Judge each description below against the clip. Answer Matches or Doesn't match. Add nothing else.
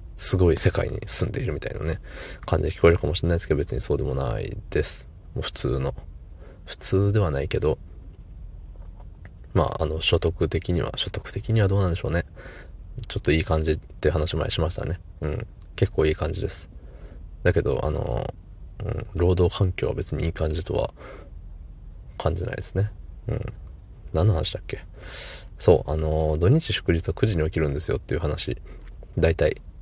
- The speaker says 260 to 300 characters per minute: Doesn't match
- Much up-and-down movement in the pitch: Doesn't match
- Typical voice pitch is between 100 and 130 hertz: Doesn't match